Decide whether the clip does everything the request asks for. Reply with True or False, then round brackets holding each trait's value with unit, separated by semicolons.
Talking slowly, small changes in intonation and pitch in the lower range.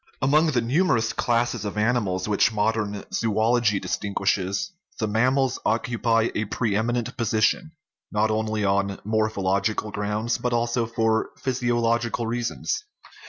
True (120 wpm; 2.2 semitones; 115 Hz)